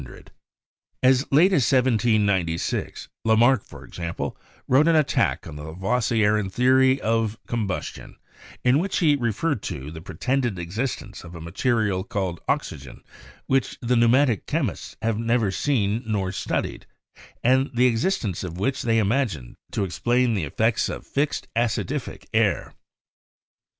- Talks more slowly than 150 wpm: Yes, average, 140 wpm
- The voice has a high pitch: No, low, 115 Hz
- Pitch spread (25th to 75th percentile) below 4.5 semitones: No, average, 5.0 semitones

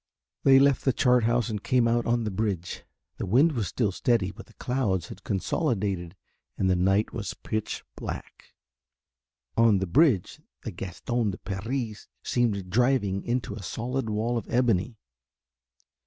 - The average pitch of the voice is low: Yes, low, 110 Hz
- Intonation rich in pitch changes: No, average, 4.0 semitones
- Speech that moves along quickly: No, average, 155 wpm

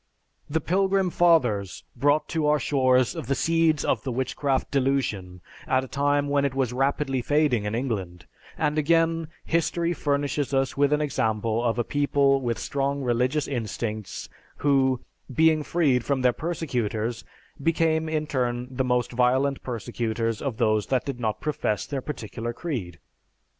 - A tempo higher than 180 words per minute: No, average, 155 wpm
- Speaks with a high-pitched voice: No, low, 135 Hz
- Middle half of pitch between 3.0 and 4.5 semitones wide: Yes, average, 3.7 semitones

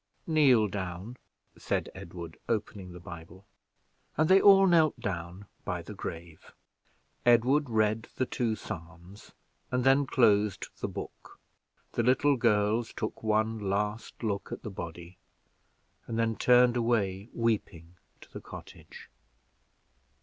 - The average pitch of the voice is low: Yes, low, 110 Hz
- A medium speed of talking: No, slow, 130 wpm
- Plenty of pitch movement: No, average, 4.6 semitones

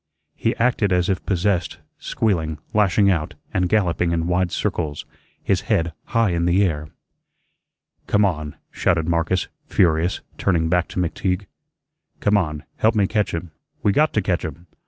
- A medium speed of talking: Yes, average, 155 wpm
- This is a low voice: Yes, very low, 90 Hz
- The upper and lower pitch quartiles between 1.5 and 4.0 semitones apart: Yes, average, 3.3 semitones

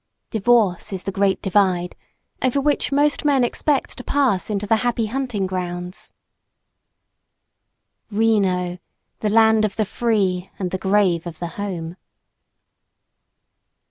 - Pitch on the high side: Yes, high, 205 Hz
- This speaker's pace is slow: Yes, slow, 125 wpm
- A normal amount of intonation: Yes, average, 4.0 semitones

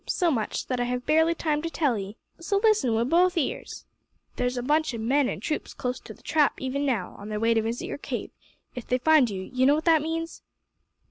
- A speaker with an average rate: No, fast, 240 wpm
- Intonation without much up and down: No, average, 4.8 semitones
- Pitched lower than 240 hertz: No, very high, 265 Hz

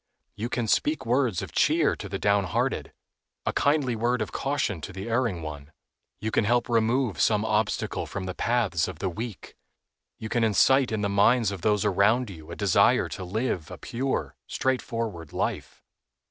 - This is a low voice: Yes, low, 110 Hz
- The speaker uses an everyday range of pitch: Yes, average, 3.8 semitones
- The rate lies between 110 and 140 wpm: No, average, 175 wpm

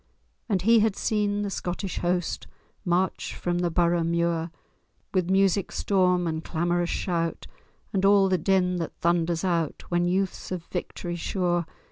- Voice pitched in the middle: Yes, medium, 175 Hz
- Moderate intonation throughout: No, narrow, 2.0 semitones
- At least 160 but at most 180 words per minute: No, average, 150 wpm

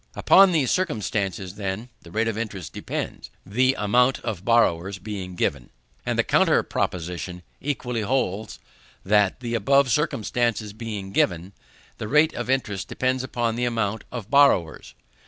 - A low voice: Yes, low, 110 Hz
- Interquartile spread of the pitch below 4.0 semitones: No, average, 4.5 semitones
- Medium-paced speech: Yes, average, 145 wpm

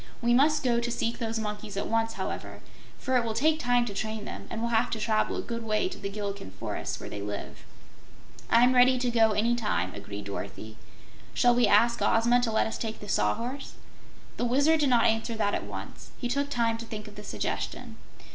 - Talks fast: Yes, fast, 220 wpm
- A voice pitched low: No, high, 230 Hz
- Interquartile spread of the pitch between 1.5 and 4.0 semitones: Yes, narrow, 2.6 semitones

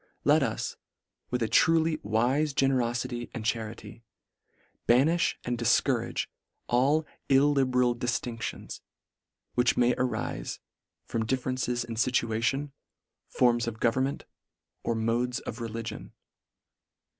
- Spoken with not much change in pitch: Yes, narrow, 2.3 semitones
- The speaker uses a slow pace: Yes, slow, 105 wpm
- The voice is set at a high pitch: No, low, 125 Hz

